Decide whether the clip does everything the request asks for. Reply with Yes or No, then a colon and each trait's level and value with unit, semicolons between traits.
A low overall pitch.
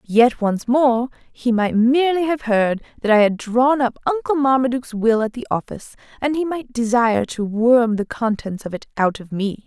No: high, 240 Hz